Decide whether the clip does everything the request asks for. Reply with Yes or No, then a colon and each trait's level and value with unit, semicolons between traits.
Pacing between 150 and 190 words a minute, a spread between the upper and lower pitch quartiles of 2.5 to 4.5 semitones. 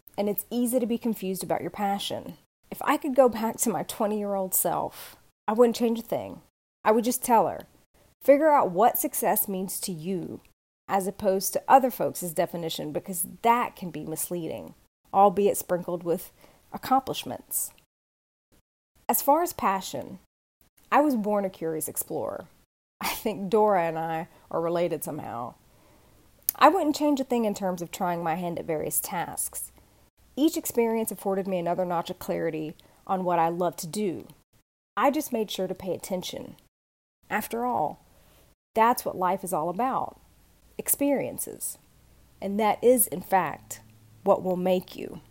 No: average, 165 wpm; average, 5.0 semitones